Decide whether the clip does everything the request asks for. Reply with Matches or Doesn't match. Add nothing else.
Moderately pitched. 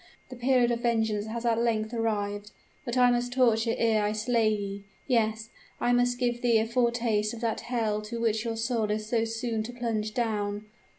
Doesn't match